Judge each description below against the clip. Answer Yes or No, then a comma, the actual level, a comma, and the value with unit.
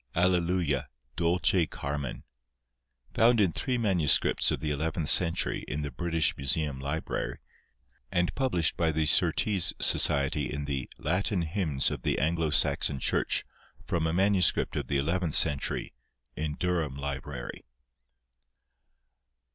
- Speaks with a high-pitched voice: No, very low, 80 Hz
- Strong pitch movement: No, average, 3.8 semitones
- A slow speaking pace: Yes, slow, 125 wpm